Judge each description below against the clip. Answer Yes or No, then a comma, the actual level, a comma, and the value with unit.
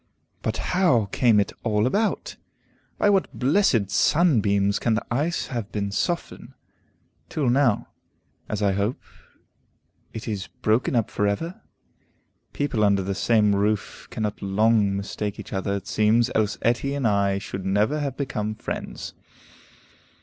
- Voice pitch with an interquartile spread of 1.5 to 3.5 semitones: No, average, 4.4 semitones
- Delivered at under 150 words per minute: Yes, average, 140 wpm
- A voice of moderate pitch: No, low, 110 Hz